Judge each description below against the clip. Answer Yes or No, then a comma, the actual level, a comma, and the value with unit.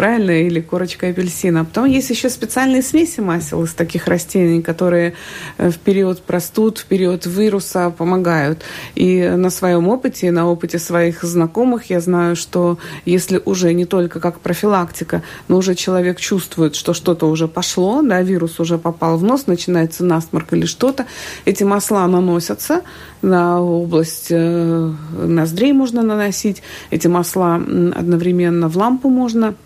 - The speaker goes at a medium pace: Yes, average, 145 wpm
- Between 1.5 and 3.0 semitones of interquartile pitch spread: Yes, average, 2.7 semitones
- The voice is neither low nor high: Yes, medium, 180 Hz